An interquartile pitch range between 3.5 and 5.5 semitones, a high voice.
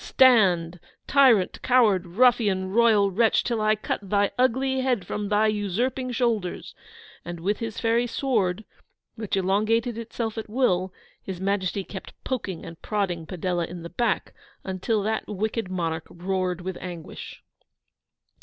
Yes: average, 4.0 semitones; high, 205 Hz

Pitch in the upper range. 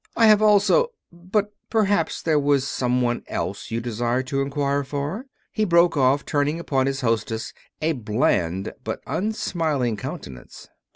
No: medium, 145 Hz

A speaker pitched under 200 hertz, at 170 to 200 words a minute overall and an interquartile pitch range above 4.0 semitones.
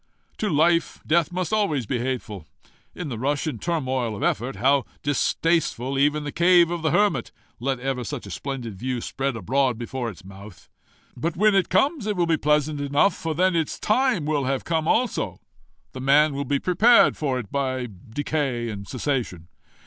Yes: medium, 140 Hz; average, 185 wpm; average, 4.8 semitones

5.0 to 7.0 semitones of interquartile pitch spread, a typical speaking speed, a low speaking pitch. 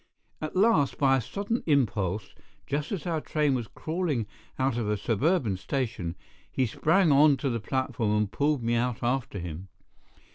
Yes: wide, 5.5 semitones; average, 170 wpm; low, 130 Hz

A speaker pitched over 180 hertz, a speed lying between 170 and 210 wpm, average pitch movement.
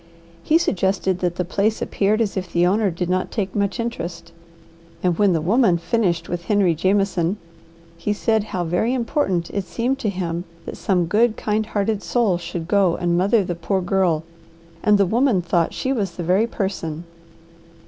Yes: high, 190 Hz; average, 180 wpm; average, 3.5 semitones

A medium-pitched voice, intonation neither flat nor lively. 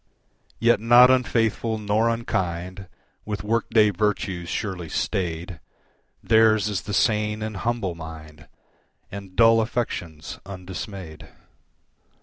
No: low, 105 Hz; average, 4.0 semitones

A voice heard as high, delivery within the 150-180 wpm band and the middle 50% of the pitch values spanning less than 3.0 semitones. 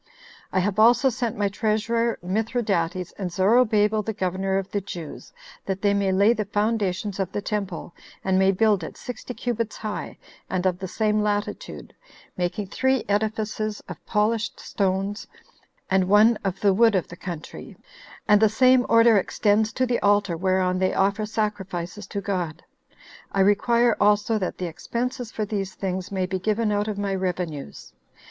Yes: high, 205 Hz; average, 165 wpm; narrow, 2.6 semitones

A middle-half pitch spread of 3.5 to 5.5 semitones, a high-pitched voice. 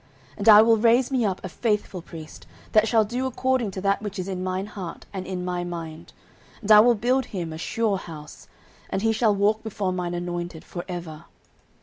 Yes: average, 4.0 semitones; high, 195 Hz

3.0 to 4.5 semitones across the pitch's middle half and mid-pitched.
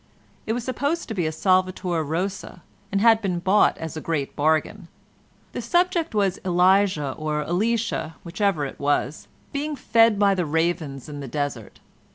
No: average, 5.3 semitones; medium, 180 Hz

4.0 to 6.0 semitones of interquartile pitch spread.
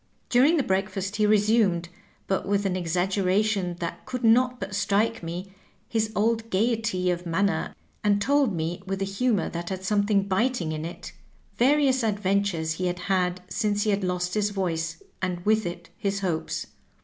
No: average, 3.2 semitones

